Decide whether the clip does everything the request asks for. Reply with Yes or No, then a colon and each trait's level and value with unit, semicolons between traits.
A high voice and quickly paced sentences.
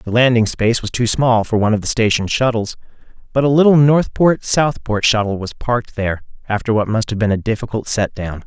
No: low, 115 Hz; fast, 215 wpm